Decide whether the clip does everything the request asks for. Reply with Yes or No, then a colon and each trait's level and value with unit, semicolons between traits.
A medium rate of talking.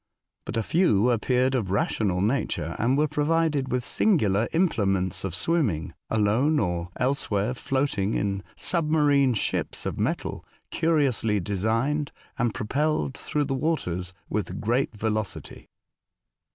No: slow, 130 wpm